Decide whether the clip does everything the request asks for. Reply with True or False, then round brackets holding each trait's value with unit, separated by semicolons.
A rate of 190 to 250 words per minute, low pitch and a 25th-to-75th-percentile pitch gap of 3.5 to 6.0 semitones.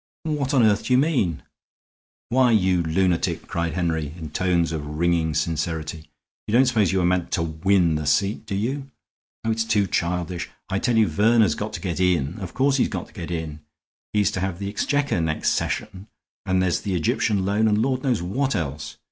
True (200 wpm; 95 Hz; 4.8 semitones)